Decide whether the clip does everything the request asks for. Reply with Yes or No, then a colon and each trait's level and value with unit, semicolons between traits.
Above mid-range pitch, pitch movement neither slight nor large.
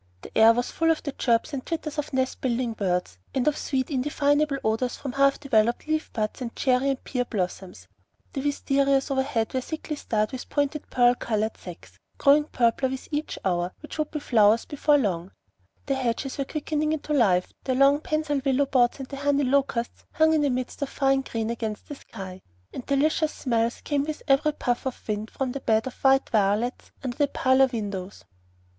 Yes: very high, 265 Hz; average, 3.8 semitones